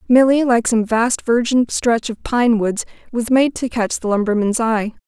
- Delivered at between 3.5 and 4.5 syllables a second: Yes, 4.4 syllables/s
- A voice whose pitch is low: No, high, 230 Hz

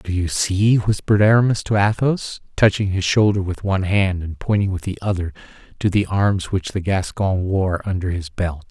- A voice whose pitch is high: No, very low, 95 Hz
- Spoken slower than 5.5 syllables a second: Yes, 5.0 syllables/s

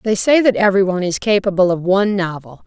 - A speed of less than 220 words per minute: Yes, fast, 205 wpm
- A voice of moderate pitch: No, high, 195 Hz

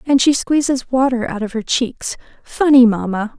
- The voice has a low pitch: No, high, 245 Hz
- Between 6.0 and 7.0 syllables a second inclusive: No, 4.7 syllables/s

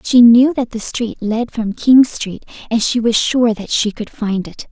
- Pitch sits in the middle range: No, high, 230 Hz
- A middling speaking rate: No, fast, 230 wpm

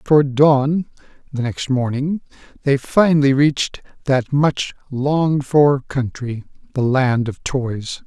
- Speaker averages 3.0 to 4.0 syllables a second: Yes, 3.8 syllables/s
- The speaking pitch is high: No, low, 135 Hz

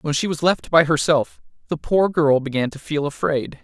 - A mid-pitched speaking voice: Yes, medium, 150 Hz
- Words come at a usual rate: No, fast, 215 wpm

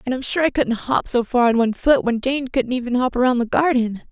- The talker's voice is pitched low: No, very high, 250 Hz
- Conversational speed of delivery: No, fast, 275 wpm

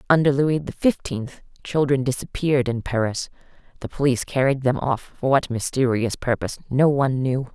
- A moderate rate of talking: Yes, average, 160 wpm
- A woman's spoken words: Yes, female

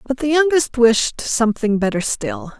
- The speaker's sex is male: No, female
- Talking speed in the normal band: Yes, average, 160 wpm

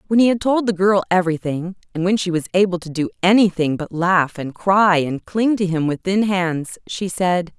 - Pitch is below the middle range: No, medium, 185 Hz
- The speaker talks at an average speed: No, fast, 220 wpm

